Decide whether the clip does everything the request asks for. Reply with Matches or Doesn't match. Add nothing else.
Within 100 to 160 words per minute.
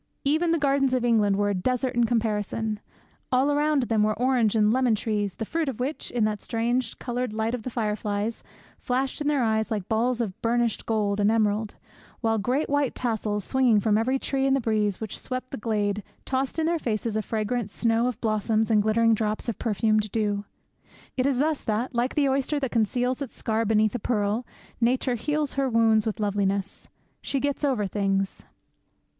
Doesn't match